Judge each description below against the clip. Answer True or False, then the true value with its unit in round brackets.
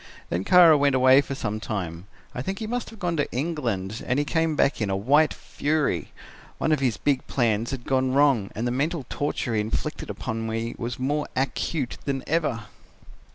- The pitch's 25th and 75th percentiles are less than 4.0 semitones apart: False (4.8 semitones)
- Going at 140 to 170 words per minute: False (200 wpm)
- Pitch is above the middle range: False (130 Hz)